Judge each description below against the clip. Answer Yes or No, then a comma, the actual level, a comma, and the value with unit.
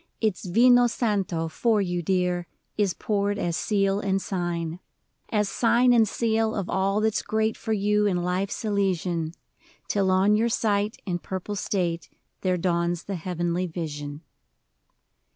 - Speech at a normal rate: Yes, average, 150 wpm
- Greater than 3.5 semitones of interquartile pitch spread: No, average, 3.2 semitones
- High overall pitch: Yes, high, 195 Hz